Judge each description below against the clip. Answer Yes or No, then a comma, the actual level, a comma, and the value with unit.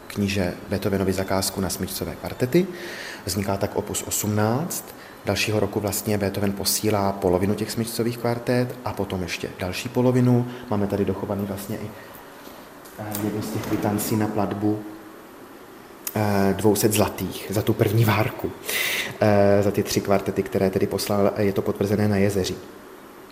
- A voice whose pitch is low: Yes, low, 105 Hz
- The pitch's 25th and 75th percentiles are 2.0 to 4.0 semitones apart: No, narrow, 1.6 semitones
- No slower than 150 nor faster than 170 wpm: No, average, 135 wpm